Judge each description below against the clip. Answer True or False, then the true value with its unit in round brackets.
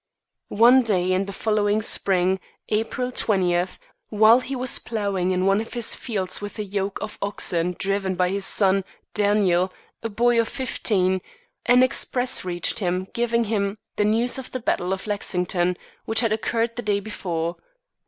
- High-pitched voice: True (205 Hz)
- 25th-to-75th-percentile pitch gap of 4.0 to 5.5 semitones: False (3.5 semitones)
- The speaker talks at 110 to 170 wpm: True (165 wpm)